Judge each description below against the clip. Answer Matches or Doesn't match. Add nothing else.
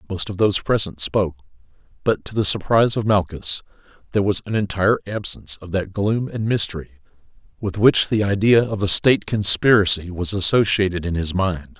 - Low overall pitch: Matches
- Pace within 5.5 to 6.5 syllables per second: Matches